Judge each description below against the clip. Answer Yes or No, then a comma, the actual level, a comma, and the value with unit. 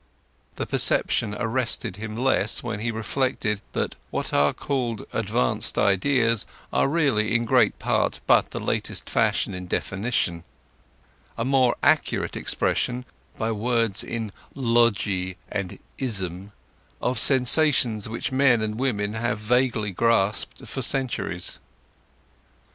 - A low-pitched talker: Yes, low, 115 Hz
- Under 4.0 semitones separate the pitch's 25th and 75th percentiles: Yes, average, 3.5 semitones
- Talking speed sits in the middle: No, slow, 120 wpm